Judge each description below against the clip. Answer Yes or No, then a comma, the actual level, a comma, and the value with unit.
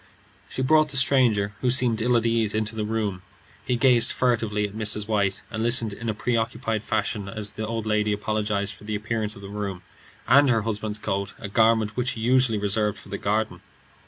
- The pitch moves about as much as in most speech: No, narrow, 2.0 semitones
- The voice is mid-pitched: No, low, 110 Hz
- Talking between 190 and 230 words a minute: Yes, average, 200 wpm